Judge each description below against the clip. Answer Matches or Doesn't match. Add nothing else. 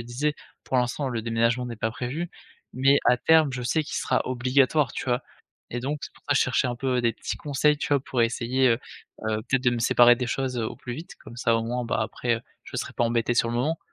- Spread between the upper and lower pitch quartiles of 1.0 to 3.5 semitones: Matches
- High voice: Doesn't match